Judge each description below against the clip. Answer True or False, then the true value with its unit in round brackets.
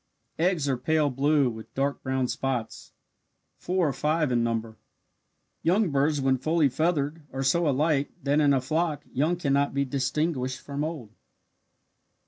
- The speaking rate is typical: True (150 wpm)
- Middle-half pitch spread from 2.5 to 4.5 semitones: True (3.0 semitones)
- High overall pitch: False (140 Hz)